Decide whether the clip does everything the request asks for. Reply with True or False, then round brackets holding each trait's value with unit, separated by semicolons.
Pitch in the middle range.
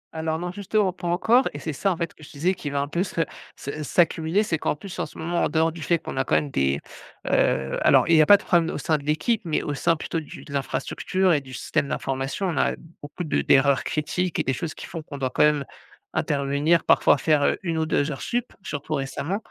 True (160 Hz)